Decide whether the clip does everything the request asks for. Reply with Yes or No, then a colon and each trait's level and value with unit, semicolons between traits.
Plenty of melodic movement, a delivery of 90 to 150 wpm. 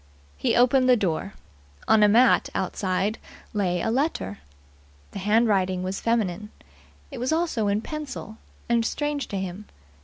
No: average, 4.6 semitones; average, 145 wpm